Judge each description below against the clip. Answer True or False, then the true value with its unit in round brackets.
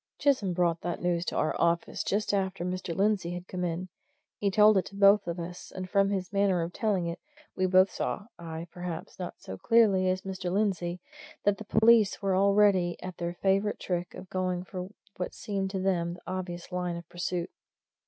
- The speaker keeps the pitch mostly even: True (2.2 semitones)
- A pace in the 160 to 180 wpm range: False (200 wpm)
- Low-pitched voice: False (185 Hz)